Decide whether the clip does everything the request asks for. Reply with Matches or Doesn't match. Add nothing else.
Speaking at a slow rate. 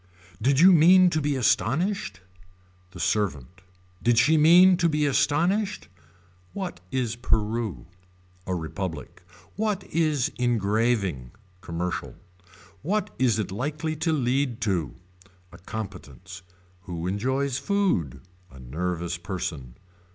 Matches